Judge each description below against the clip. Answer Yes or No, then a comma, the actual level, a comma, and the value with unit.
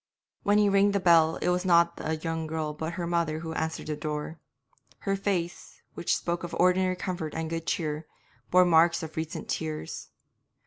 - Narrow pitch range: Yes, narrow, 2.1 semitones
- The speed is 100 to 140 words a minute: No, average, 185 wpm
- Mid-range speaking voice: Yes, medium, 165 Hz